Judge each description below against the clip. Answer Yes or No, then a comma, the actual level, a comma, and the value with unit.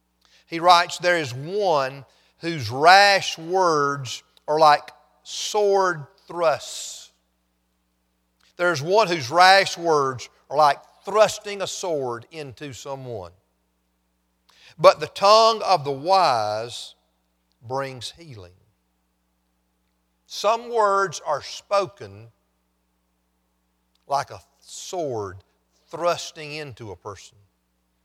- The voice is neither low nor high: No, low, 130 Hz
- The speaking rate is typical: No, slow, 95 wpm